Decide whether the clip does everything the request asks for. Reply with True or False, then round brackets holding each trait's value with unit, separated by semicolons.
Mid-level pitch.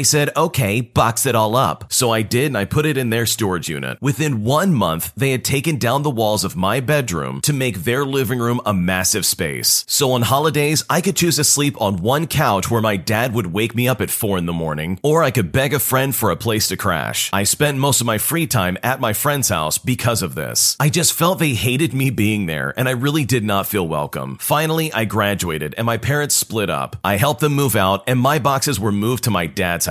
False (125 Hz)